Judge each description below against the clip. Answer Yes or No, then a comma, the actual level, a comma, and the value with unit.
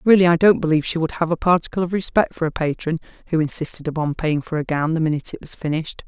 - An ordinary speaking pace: No, fast, 255 wpm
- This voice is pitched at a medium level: Yes, medium, 160 Hz